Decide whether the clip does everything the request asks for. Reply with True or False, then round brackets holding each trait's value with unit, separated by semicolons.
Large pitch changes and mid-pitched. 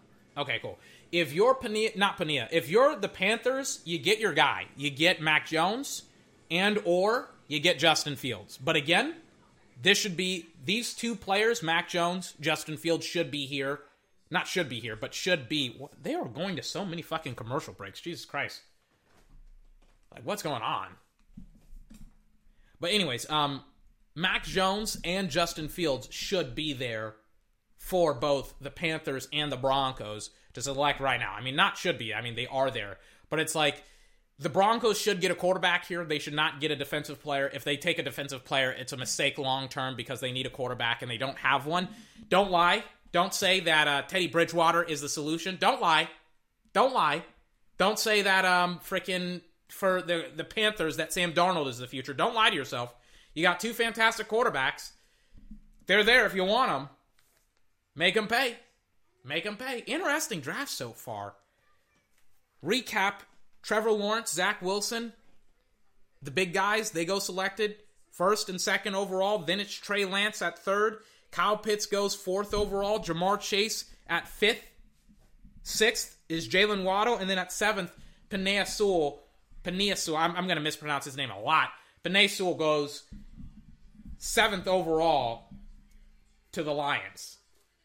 True (6.0 semitones; 170 Hz)